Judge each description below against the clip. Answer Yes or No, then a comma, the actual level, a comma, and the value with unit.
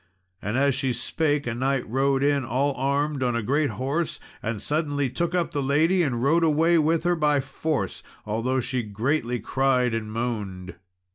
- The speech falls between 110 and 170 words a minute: No, average, 180 wpm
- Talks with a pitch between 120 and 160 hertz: Yes, low, 135 Hz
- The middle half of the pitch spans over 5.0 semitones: No, average, 3.8 semitones